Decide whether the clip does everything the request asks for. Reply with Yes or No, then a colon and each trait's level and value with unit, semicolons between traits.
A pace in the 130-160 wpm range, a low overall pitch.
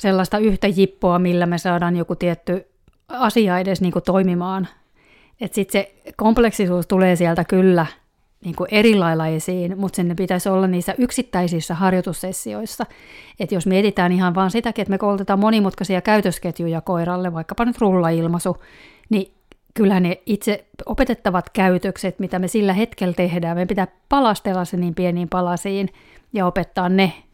No: average, 145 wpm; medium, 185 Hz